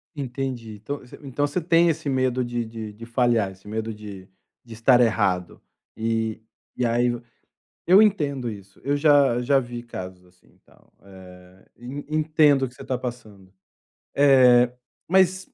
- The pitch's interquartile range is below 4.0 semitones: No, average, 4.5 semitones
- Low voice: Yes, low, 120 Hz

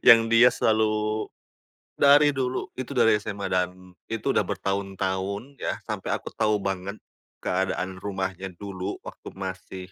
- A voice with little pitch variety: No, average, 3.0 semitones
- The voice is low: Yes, low, 100 Hz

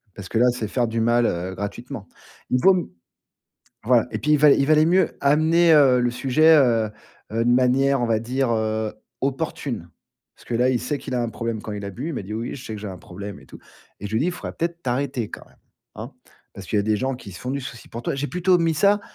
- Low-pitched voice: Yes, low, 125 Hz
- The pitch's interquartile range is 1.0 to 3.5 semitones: No, average, 4.5 semitones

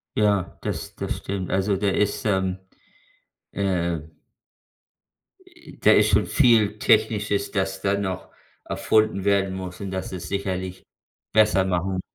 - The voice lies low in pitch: Yes, very low, 95 Hz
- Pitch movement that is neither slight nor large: No, narrow, 1.8 semitones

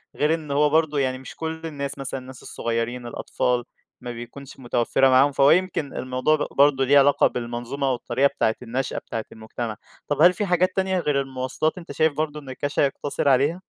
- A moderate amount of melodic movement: Yes, average, 3.0 semitones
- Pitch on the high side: No, medium, 140 Hz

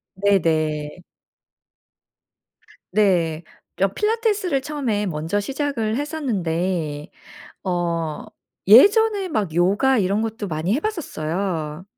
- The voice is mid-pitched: No, high, 200 Hz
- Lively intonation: Yes, wide, 8.6 semitones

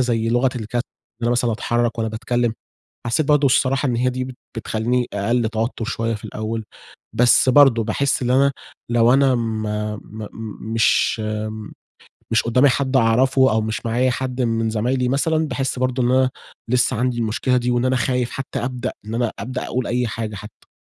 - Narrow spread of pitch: Yes, narrow, 2.1 semitones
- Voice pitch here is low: Yes, low, 120 Hz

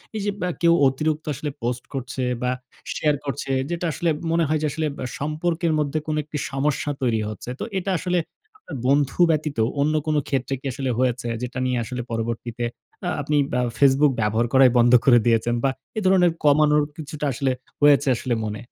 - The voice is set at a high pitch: No, medium, 140 Hz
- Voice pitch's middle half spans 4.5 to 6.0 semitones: No, average, 3.6 semitones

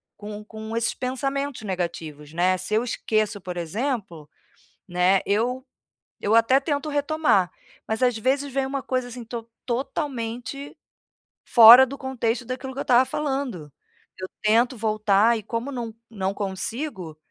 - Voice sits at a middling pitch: No, high, 230 Hz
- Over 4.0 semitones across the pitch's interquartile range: Yes, average, 4.7 semitones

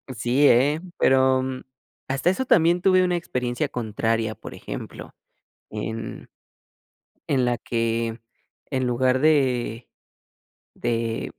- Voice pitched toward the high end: No, low, 125 Hz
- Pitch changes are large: No, average, 3.8 semitones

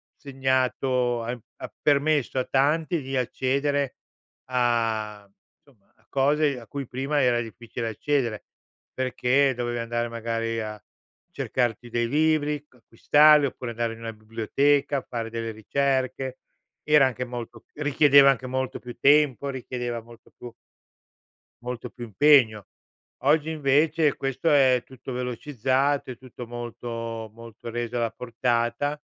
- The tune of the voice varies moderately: Yes, average, 3.2 semitones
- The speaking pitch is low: Yes, low, 125 Hz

